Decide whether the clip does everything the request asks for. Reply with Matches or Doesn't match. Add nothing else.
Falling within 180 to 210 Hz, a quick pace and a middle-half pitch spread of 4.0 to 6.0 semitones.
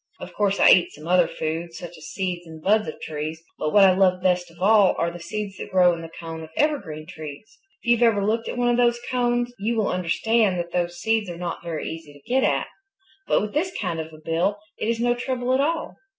Matches